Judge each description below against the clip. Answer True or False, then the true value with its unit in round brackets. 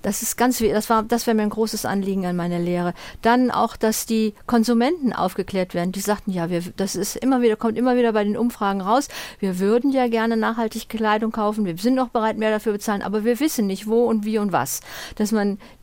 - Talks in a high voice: True (215 Hz)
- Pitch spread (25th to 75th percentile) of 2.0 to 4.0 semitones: True (2.8 semitones)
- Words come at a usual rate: False (235 wpm)